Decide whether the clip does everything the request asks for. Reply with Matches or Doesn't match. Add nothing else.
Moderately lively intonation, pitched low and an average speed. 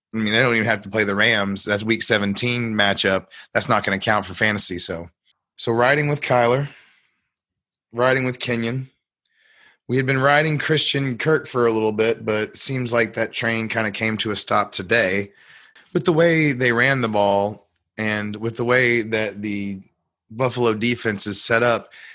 Matches